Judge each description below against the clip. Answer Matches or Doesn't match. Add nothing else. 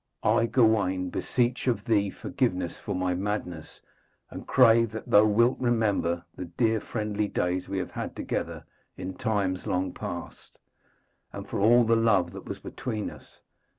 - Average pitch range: Matches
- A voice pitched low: Matches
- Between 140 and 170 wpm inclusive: Matches